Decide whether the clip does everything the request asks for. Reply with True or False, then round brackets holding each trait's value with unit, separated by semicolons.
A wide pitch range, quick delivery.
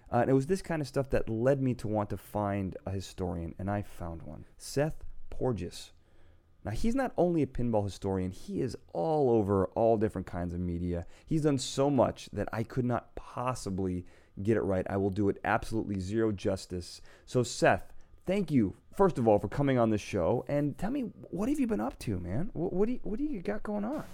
True (7.0 semitones; 225 wpm)